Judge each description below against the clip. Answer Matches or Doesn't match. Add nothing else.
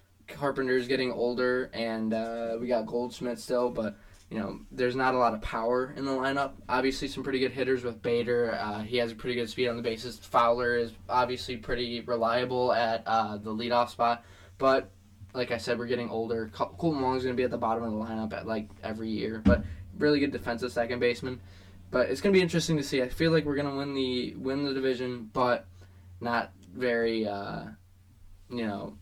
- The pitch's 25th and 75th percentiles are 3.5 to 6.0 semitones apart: Doesn't match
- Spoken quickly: Matches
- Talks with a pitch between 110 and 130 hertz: Matches